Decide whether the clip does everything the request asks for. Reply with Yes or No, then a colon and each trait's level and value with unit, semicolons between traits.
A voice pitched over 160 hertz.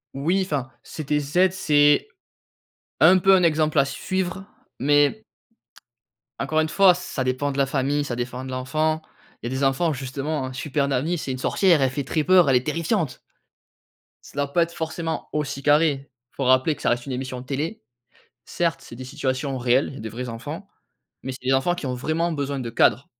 No: medium, 145 Hz